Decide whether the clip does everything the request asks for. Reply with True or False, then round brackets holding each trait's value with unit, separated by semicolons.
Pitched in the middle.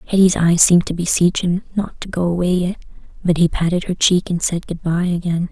True (175 Hz)